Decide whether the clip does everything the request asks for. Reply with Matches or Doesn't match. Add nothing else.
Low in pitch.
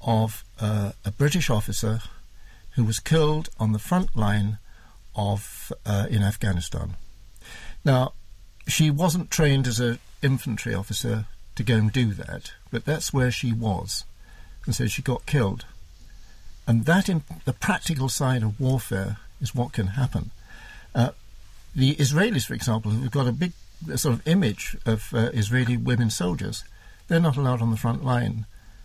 Matches